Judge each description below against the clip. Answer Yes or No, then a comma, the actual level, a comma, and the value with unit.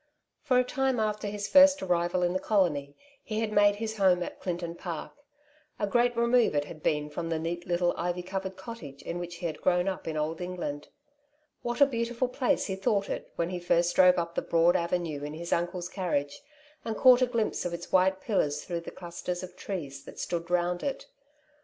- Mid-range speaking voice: Yes, medium, 180 Hz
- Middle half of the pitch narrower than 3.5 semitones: No, average, 3.8 semitones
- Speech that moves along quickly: Yes, fast, 210 wpm